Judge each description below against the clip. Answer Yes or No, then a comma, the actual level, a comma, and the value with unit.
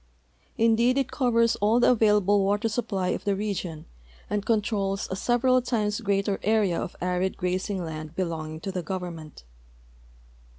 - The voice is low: No, high, 200 Hz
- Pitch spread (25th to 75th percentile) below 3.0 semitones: No, average, 3.7 semitones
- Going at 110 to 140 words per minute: No, average, 155 wpm